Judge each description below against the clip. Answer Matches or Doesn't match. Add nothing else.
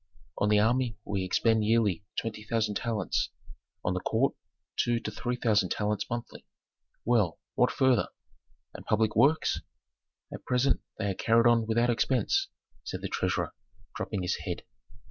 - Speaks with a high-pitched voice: Doesn't match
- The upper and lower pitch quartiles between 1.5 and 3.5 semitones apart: Matches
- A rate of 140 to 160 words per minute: Matches